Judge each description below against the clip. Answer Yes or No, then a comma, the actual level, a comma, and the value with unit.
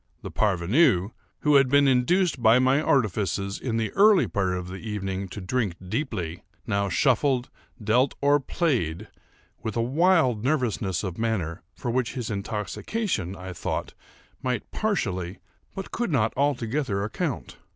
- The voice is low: Yes, low, 115 Hz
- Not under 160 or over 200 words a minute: No, average, 145 wpm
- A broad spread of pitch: Yes, wide, 6.0 semitones